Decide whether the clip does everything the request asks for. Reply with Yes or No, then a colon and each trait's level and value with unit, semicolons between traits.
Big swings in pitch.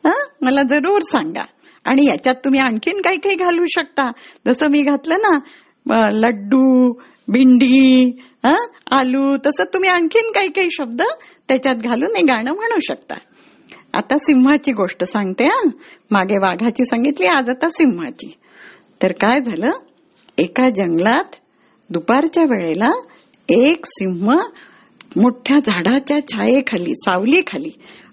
No: average, 4.9 semitones